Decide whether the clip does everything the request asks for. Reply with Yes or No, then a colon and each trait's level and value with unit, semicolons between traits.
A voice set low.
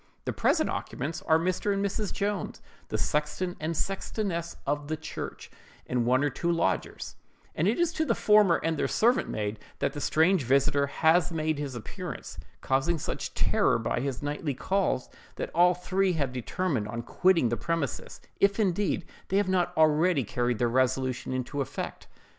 No: medium, 155 Hz